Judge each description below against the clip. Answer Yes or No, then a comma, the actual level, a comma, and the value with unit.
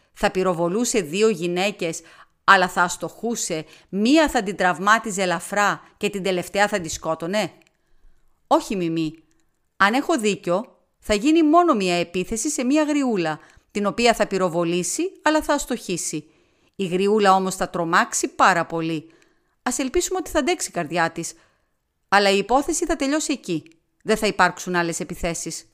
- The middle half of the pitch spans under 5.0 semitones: No, wide, 5.6 semitones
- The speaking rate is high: No, average, 150 wpm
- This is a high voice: Yes, high, 195 Hz